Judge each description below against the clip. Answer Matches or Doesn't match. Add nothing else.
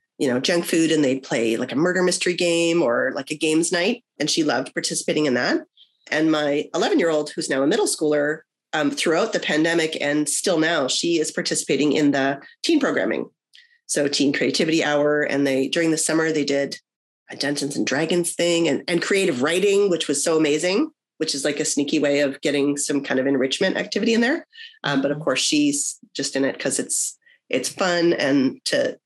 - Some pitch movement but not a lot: Matches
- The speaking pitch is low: Doesn't match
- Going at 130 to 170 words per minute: Doesn't match